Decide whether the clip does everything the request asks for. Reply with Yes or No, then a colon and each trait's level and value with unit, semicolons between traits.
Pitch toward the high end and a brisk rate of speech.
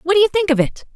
Yes: very high, 340 Hz; fast, 380 wpm